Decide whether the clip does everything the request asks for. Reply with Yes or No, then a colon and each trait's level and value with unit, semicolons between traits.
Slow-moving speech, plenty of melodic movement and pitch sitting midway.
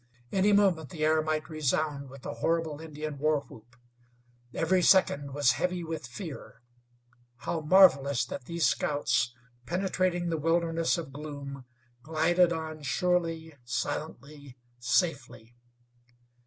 No: slow, 120 wpm; average, 3.2 semitones; medium, 155 Hz